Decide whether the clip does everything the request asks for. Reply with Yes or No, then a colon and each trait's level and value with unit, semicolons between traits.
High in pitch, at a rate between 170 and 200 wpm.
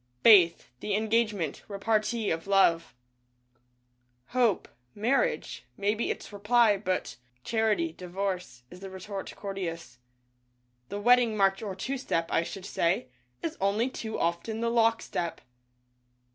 No: high, 200 Hz; average, 145 wpm